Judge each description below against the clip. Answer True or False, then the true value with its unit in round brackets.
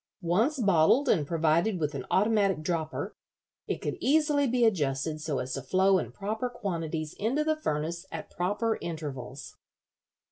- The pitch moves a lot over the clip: True (6.2 semitones)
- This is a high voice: False (175 Hz)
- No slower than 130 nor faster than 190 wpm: True (150 wpm)